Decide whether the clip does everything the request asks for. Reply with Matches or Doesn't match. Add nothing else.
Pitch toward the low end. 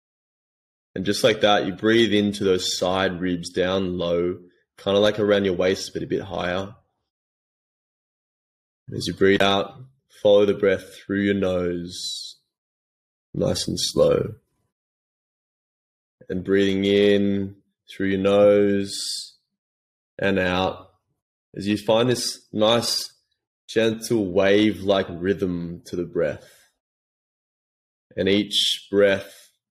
Matches